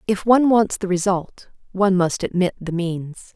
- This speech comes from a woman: Yes, female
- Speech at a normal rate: Yes, average, 180 wpm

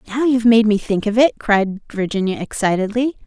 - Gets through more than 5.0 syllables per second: Yes, 5.5 syllables/s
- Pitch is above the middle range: Yes, high, 215 Hz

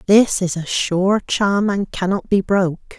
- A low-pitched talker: No, high, 195 Hz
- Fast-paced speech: No, average, 180 wpm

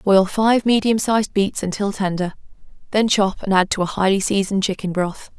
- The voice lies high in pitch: Yes, high, 200 Hz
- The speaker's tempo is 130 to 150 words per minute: No, average, 190 wpm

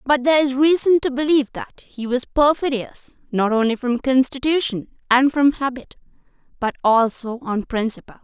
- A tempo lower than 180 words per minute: Yes, average, 155 wpm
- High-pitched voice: Yes, very high, 260 Hz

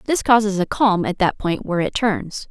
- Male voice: No, female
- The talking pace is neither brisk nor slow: No, fast, 240 wpm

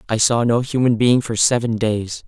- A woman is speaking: No, male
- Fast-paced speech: Yes, fast, 210 wpm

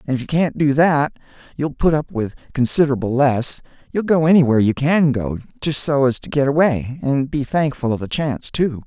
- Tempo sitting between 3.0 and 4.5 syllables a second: No, 5.5 syllables/s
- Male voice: Yes, male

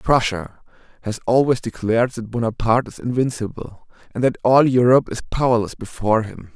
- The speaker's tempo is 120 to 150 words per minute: Yes, average, 145 wpm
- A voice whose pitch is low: Yes, low, 115 Hz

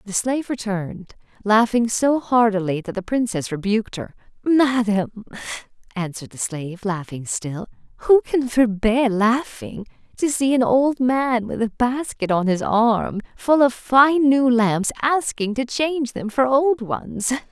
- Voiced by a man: No, female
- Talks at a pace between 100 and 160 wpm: Yes, average, 150 wpm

